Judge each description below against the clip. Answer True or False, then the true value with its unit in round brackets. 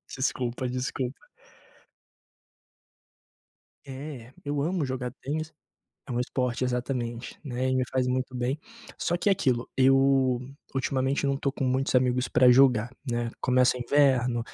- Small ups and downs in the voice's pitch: True (1.6 semitones)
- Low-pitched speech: True (130 Hz)